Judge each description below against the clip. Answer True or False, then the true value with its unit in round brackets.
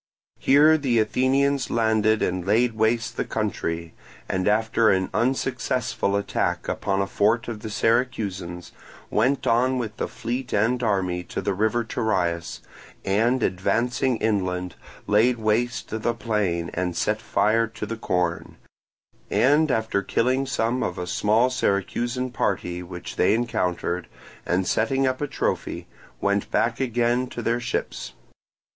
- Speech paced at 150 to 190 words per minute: False (140 wpm)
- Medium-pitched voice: False (110 Hz)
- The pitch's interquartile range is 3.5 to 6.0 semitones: True (3.8 semitones)